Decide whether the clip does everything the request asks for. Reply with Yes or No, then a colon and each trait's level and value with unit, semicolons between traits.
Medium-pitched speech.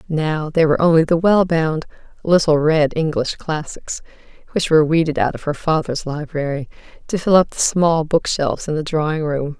Yes: medium, 155 Hz